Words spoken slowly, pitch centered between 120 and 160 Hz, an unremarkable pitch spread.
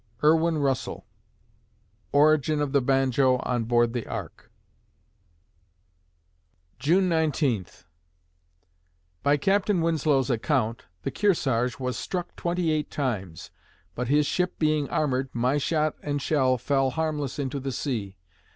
Yes: slow, 120 wpm; medium, 140 Hz; average, 3.5 semitones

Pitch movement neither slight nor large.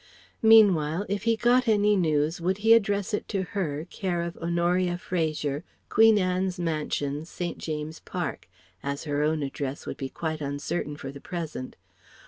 Yes: average, 4.6 semitones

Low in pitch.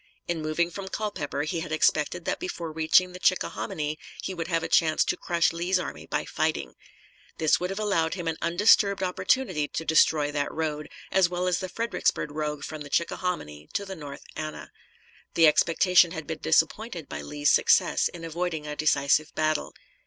No: medium, 165 Hz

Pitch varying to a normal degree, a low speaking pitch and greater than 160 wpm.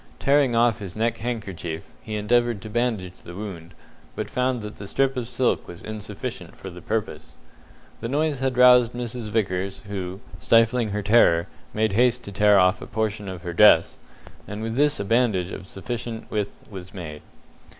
Yes: average, 3.9 semitones; low, 110 Hz; average, 180 wpm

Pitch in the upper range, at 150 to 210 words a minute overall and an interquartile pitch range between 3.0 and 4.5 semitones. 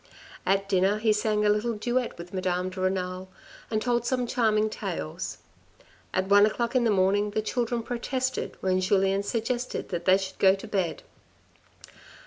Yes: high, 205 Hz; average, 165 wpm; average, 3.6 semitones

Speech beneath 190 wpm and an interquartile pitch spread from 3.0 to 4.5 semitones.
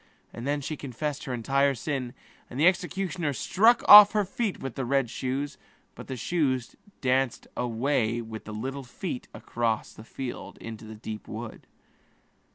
Yes: average, 165 wpm; average, 3.9 semitones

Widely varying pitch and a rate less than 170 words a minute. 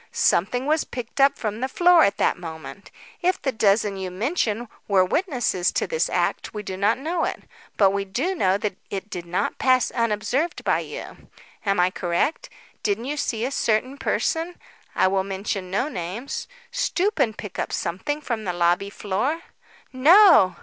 No: wide, 6.7 semitones; average, 180 wpm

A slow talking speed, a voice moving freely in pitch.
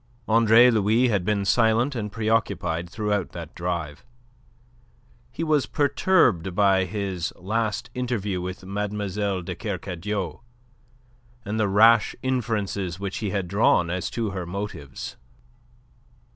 No: slow, 120 wpm; average, 3.4 semitones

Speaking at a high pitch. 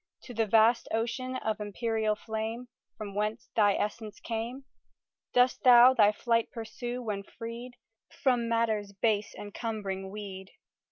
Yes: high, 225 Hz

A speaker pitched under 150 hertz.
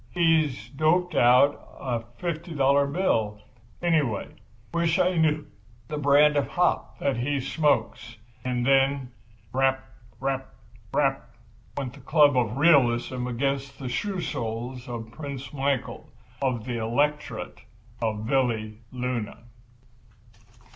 Yes: low, 135 Hz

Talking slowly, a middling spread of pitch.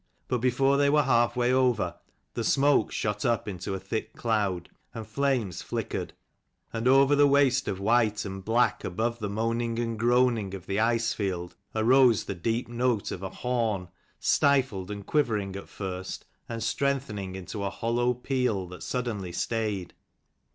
No: average, 165 wpm; average, 4.0 semitones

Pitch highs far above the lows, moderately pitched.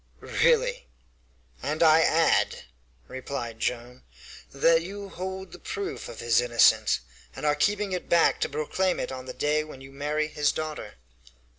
Yes: wide, 6.0 semitones; medium, 155 Hz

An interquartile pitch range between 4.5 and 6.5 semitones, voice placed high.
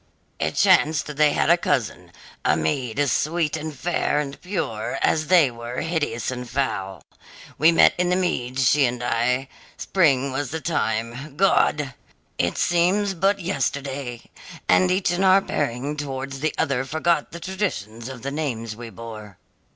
No: average, 5.3 semitones; medium, 140 Hz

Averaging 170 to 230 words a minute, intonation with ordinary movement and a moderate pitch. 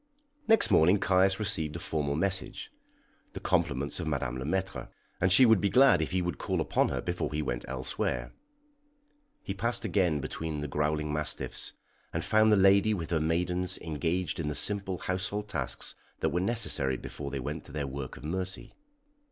No: average, 185 wpm; average, 4.4 semitones; very low, 85 Hz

